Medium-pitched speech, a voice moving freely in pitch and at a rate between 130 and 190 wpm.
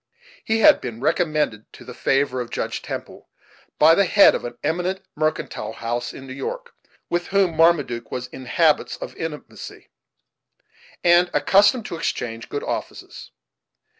Yes: medium, 155 Hz; wide, 5.9 semitones; average, 150 wpm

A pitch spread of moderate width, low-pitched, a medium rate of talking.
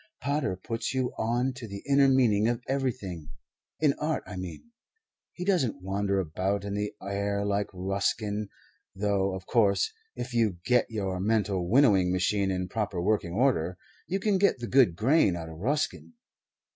Yes: average, 4.9 semitones; low, 105 Hz; average, 165 wpm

